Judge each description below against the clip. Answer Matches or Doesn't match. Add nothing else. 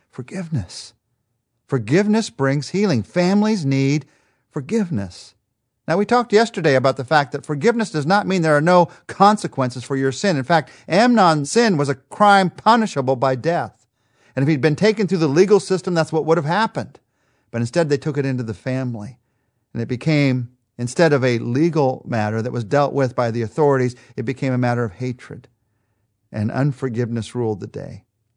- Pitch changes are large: Matches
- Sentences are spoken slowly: Doesn't match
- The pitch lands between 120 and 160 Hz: Matches